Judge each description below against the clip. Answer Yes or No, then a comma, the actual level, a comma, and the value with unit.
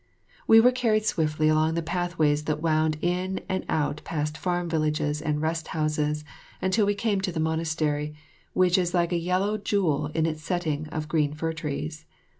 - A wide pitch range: No, average, 2.9 semitones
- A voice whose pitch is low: No, medium, 160 Hz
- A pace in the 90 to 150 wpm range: No, average, 180 wpm